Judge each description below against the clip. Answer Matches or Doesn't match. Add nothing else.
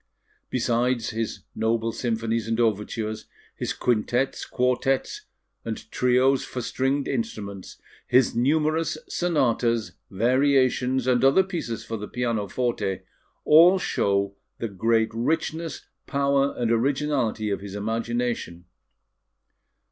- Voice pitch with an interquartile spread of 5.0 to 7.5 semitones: Doesn't match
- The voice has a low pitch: Matches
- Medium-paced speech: Doesn't match